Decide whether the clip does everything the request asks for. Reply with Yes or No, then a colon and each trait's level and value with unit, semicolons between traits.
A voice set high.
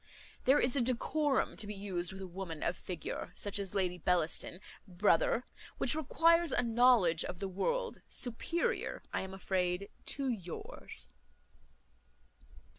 Yes: high, 200 Hz